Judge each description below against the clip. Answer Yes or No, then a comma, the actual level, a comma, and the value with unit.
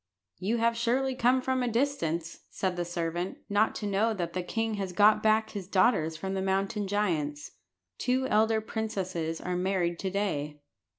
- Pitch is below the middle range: No, high, 195 Hz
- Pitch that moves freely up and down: No, average, 4.2 semitones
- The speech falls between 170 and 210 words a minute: Yes, average, 180 wpm